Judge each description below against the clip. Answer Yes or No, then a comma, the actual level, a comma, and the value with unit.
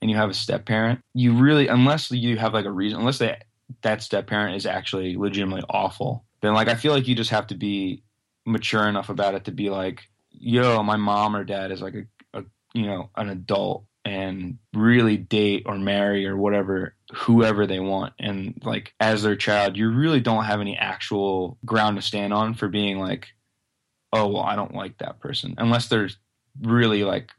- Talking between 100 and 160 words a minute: No, average, 200 wpm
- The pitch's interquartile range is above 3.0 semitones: No, average, 2.7 semitones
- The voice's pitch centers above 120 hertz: No, low, 105 Hz